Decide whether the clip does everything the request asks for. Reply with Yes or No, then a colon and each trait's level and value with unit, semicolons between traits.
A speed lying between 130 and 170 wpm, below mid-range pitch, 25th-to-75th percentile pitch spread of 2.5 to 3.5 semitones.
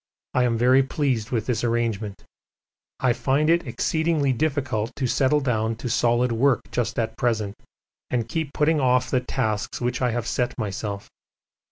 Yes: average, 165 wpm; low, 125 Hz; average, 2.9 semitones